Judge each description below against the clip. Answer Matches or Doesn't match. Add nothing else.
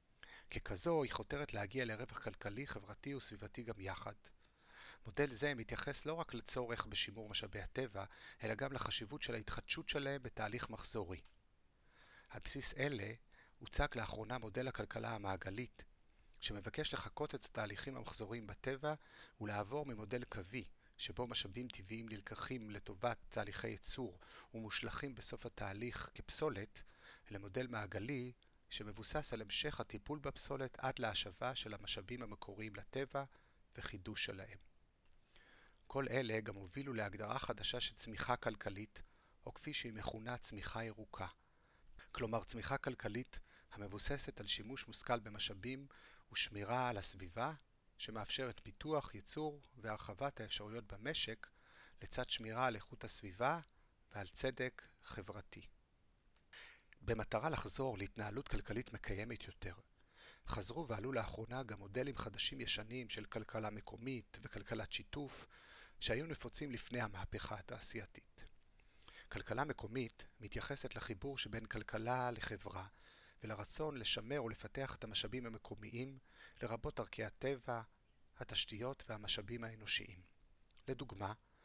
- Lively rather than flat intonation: Doesn't match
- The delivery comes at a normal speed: Matches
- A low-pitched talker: Matches